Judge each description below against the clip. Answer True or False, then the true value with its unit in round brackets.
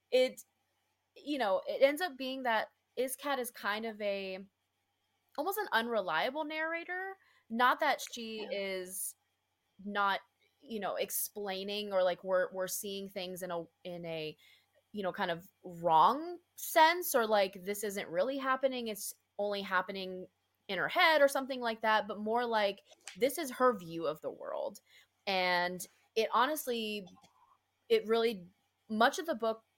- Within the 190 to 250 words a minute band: False (155 wpm)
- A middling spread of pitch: False (6.0 semitones)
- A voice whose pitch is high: True (215 Hz)